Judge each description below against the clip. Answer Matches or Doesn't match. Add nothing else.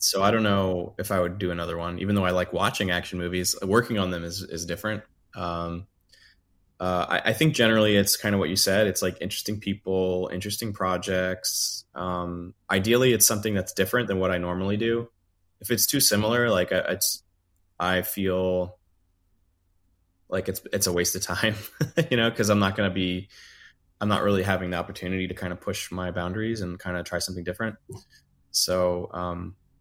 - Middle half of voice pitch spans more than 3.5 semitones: Doesn't match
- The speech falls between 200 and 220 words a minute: Doesn't match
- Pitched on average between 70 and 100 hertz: Matches